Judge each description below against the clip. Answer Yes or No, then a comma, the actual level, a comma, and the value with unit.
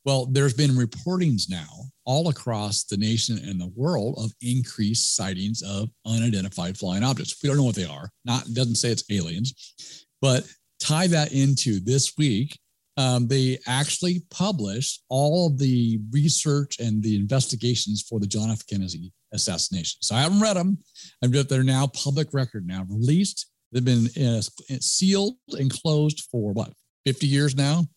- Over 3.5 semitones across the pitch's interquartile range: Yes, average, 4.9 semitones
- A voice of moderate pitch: No, low, 130 Hz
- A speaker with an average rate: Yes, average, 165 wpm